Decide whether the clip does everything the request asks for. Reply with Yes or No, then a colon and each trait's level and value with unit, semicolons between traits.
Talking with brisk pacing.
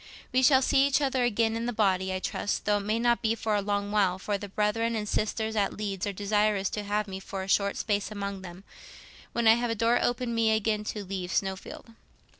Yes: fast, 235 wpm